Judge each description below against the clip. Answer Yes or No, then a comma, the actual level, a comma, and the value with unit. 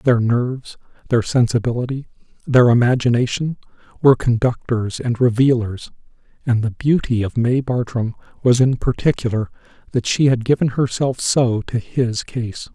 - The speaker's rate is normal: No, slow, 130 wpm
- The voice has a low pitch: Yes, low, 125 Hz